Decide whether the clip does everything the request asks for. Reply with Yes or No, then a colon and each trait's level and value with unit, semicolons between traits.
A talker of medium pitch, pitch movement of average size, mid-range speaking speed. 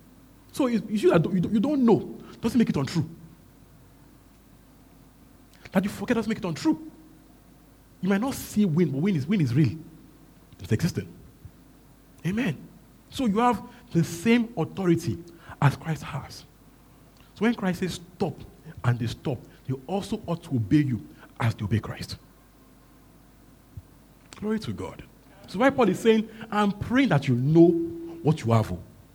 No: medium, 170 Hz; wide, 7.7 semitones; average, 150 wpm